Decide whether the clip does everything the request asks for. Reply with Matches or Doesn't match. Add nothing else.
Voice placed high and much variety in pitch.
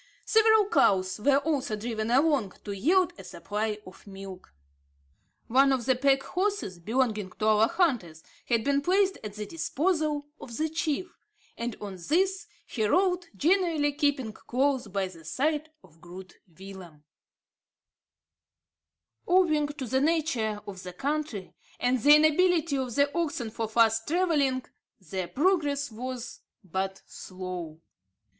Matches